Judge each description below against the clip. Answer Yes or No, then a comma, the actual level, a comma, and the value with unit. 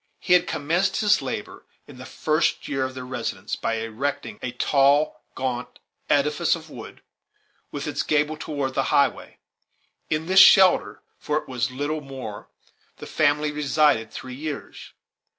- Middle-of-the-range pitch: Yes, medium, 145 Hz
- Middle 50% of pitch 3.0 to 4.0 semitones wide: Yes, average, 3.3 semitones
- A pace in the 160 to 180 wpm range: No, average, 150 wpm